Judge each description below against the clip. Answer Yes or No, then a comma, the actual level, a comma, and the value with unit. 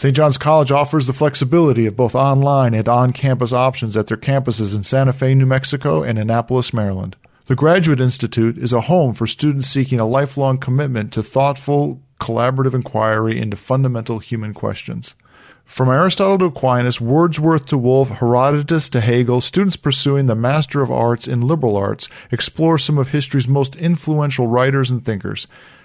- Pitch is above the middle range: No, low, 130 Hz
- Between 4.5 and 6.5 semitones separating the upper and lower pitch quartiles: No, average, 3.3 semitones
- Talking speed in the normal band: Yes, average, 165 wpm